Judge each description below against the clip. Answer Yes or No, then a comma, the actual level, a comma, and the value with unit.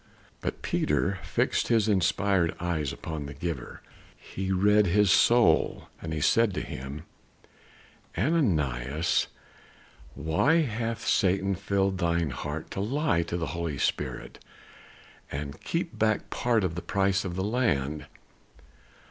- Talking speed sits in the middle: No, slow, 130 wpm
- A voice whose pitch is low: Yes, very low, 95 Hz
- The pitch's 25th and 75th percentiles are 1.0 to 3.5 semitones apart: No, average, 5.0 semitones